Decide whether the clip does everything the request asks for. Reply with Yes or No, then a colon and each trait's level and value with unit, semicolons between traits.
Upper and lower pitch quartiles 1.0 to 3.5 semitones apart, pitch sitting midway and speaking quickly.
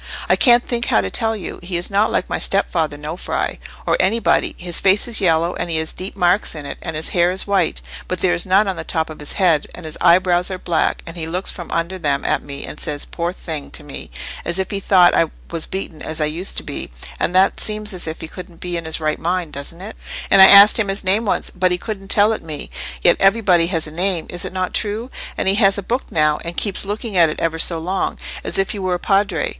Yes: average, 3.1 semitones; medium, 180 Hz; fast, 260 wpm